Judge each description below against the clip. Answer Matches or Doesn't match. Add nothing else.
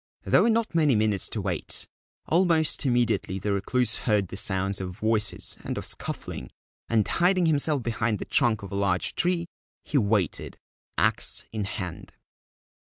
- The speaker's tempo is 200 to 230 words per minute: Doesn't match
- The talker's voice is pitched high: Doesn't match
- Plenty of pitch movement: Matches